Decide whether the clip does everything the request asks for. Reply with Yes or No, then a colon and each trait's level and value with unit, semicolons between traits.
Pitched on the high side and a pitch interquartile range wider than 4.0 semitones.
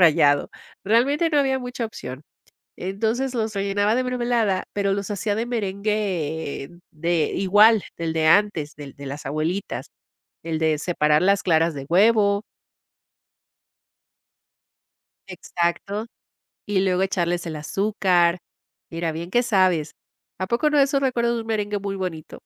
Yes: high, 195 Hz; average, 4.9 semitones